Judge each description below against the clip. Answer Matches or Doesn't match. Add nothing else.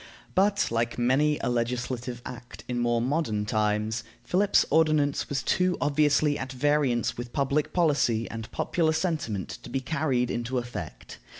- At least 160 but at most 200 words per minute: Doesn't match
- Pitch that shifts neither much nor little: Matches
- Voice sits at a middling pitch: Doesn't match